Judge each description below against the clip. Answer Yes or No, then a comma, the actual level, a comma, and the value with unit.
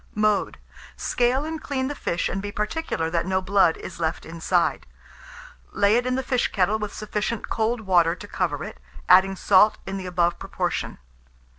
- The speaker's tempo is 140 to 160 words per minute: No, average, 175 wpm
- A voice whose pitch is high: Yes, high, 200 Hz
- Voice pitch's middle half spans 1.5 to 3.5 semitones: No, average, 4.5 semitones